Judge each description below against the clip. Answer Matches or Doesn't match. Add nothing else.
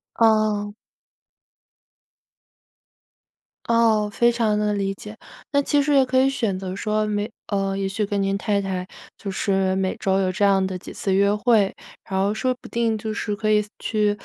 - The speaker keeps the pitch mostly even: Matches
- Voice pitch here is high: Matches